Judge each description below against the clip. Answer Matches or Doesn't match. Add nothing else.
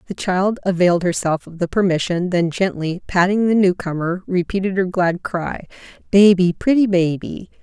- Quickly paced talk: Doesn't match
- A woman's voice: Matches